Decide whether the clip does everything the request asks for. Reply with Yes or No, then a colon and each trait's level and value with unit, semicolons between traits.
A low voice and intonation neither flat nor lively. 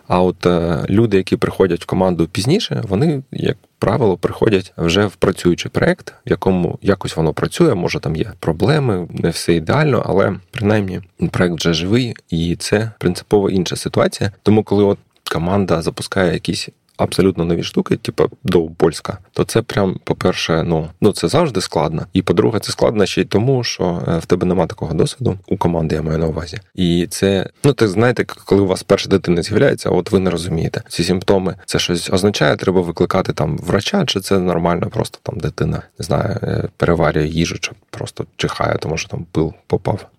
Yes: very low, 95 Hz; average, 3.6 semitones